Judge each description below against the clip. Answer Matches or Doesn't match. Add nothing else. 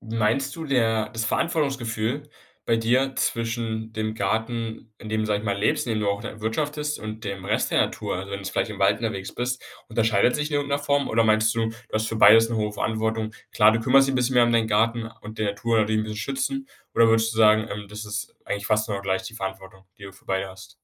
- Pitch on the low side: Matches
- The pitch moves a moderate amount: Doesn't match